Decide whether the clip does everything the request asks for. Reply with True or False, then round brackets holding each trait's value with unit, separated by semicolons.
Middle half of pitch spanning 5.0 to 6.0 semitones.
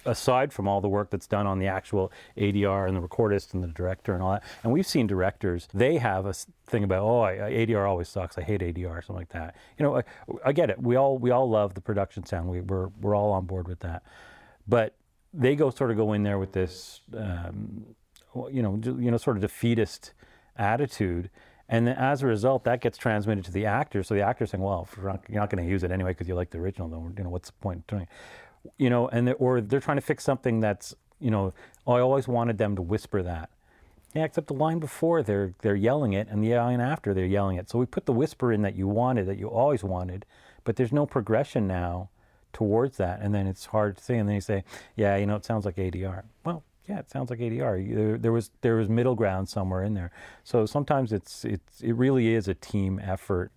False (4.0 semitones)